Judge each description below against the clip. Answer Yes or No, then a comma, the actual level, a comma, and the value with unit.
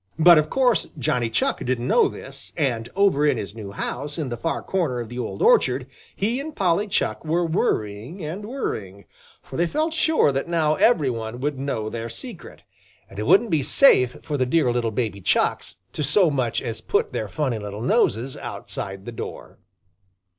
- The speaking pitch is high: No, medium, 140 Hz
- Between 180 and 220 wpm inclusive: Yes, average, 190 wpm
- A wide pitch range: Yes, wide, 7.1 semitones